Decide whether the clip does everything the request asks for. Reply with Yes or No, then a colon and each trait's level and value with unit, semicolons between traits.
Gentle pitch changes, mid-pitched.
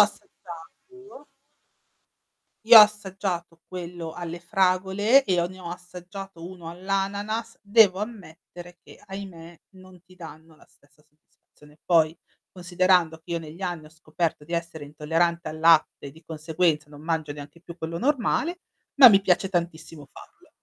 No: average, 3.0 semitones; medium, 175 Hz